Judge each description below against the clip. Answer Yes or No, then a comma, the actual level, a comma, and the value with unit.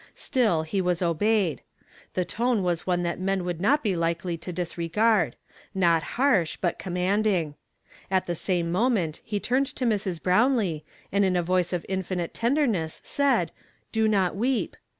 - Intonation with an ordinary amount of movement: Yes, average, 4.1 semitones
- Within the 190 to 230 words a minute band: No, average, 170 wpm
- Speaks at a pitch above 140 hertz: Yes, medium, 185 Hz